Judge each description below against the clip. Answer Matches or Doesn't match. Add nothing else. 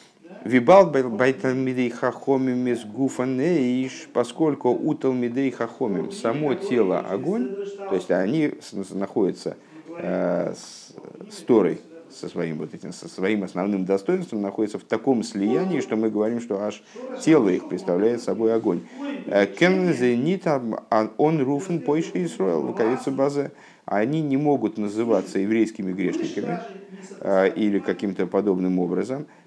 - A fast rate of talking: Doesn't match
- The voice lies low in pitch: Matches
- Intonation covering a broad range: Matches